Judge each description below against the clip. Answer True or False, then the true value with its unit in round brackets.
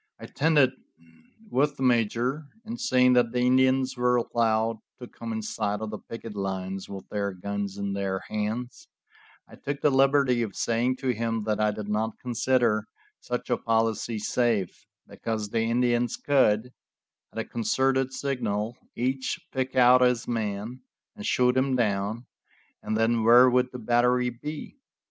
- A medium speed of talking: True (160 wpm)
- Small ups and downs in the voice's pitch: False (3.0 semitones)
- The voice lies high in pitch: False (120 Hz)